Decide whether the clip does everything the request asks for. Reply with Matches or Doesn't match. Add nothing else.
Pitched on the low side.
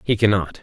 Matches